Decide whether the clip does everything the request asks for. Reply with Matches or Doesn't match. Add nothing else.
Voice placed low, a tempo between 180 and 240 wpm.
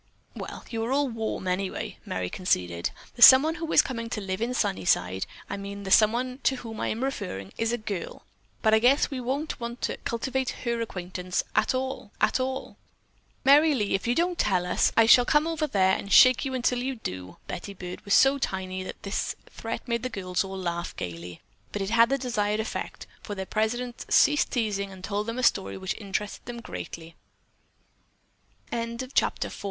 Doesn't match